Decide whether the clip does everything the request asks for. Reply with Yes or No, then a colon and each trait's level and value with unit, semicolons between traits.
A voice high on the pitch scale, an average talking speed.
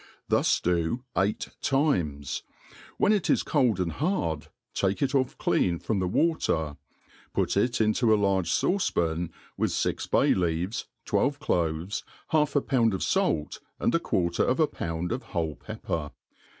No: very low, 95 Hz; average, 160 wpm